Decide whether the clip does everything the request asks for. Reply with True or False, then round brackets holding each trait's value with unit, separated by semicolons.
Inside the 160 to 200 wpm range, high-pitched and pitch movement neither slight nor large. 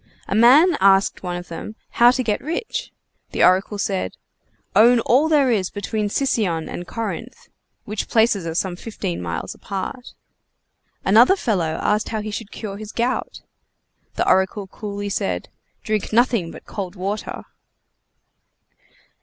False (145 wpm; 210 Hz; 3.9 semitones)